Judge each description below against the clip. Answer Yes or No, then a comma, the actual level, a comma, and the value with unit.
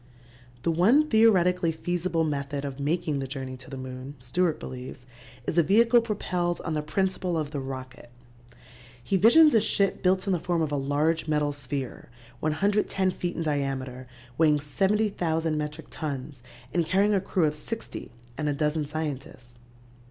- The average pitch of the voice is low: No, medium, 155 Hz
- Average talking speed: Yes, average, 165 wpm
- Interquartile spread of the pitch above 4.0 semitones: Yes, average, 4.6 semitones